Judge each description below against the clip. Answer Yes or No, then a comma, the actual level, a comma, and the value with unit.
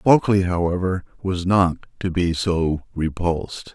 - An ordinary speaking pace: No, slow, 130 wpm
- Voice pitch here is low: Yes, very low, 90 Hz